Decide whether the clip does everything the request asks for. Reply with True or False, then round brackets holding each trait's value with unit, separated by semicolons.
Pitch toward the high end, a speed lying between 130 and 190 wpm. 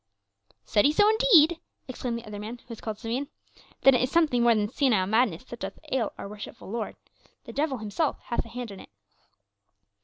False (240 Hz; 205 wpm)